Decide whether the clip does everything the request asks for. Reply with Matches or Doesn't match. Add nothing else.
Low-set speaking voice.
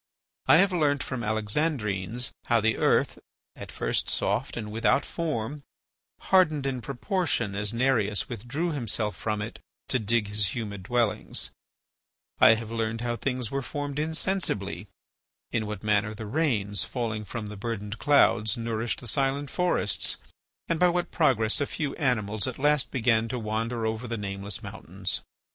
Matches